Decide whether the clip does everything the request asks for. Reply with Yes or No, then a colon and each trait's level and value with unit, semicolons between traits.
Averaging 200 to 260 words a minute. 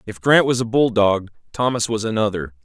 No: average, 180 wpm